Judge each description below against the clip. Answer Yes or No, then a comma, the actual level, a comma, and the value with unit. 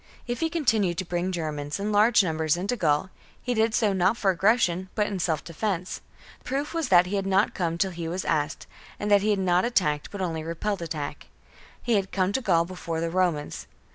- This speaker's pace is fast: Yes, fast, 220 wpm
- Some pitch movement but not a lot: Yes, average, 3.8 semitones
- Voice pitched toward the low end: No, medium, 185 Hz